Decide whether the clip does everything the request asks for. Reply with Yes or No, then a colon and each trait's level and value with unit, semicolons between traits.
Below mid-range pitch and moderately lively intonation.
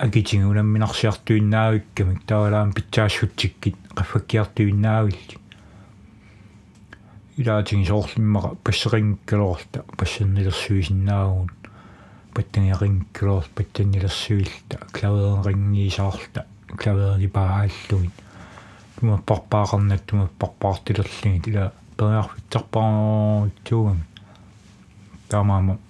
No: low, 105 Hz; narrow, 1.5 semitones